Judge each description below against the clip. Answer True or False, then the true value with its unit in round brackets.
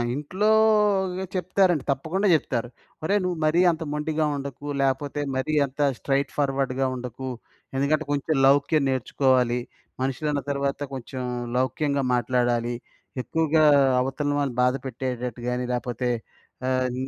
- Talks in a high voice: False (140 Hz)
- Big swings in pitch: False (3.5 semitones)